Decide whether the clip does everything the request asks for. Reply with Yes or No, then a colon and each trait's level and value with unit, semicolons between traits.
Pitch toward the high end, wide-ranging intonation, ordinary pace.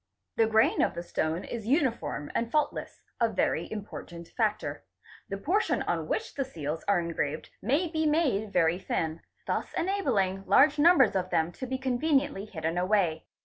Yes: high, 215 Hz; wide, 8.1 semitones; average, 170 wpm